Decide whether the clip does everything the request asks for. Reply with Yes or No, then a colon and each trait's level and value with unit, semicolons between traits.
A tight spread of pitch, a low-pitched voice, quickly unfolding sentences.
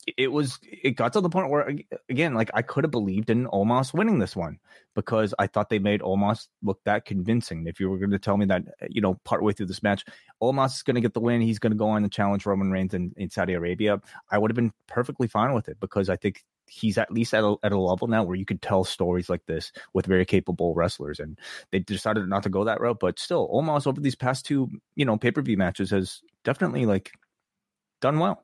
No: average, 3.8 semitones; low, 105 Hz; fast, 255 wpm